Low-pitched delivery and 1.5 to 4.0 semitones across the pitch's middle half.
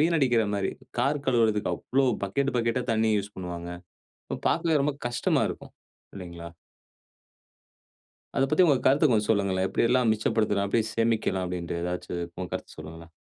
No: low, 110 Hz; average, 5.3 semitones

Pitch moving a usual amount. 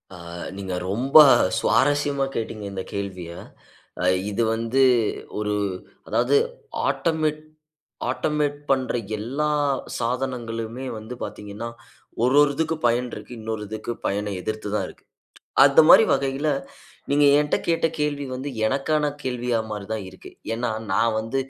Yes: average, 4.6 semitones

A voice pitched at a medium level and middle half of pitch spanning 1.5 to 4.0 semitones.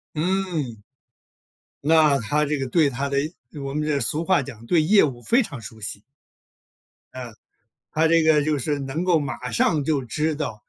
Yes: medium, 150 Hz; average, 3.6 semitones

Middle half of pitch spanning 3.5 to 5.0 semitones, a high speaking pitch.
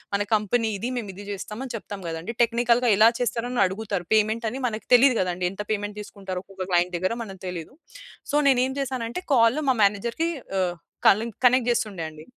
Yes: average, 3.8 semitones; high, 215 Hz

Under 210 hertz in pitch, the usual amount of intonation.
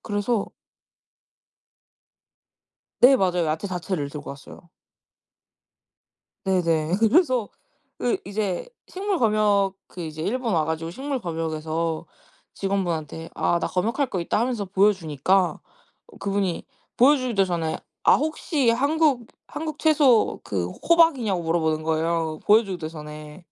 No: high, 190 Hz; wide, 6.6 semitones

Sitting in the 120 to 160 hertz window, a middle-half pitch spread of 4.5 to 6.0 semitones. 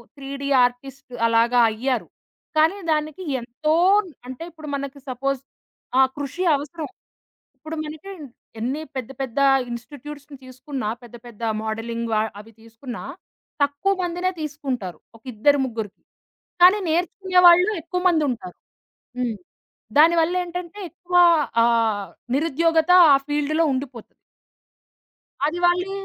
No: very high, 280 Hz; average, 5.2 semitones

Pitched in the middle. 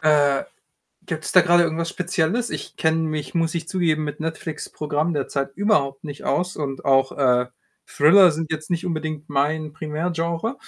Yes: medium, 155 Hz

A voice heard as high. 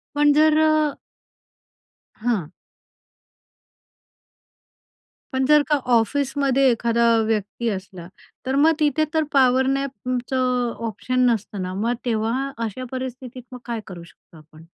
Yes: very high, 250 Hz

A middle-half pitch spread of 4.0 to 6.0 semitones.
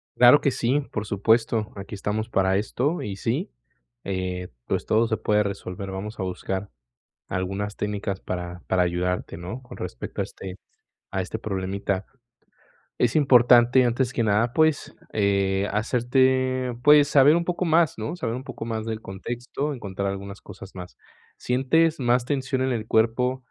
Yes: average, 4.7 semitones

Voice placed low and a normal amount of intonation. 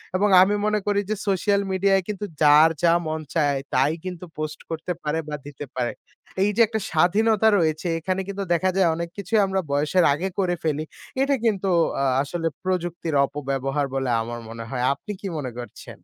No: medium, 170 Hz; average, 4.8 semitones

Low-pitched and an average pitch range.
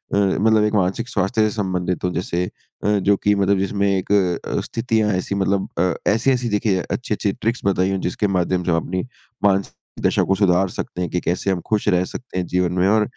No: very low, 95 Hz; narrow, 2.3 semitones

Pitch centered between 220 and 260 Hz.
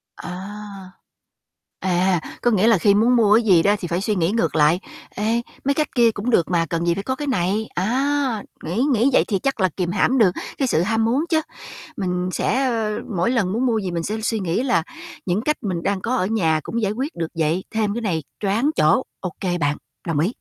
No: high, 205 Hz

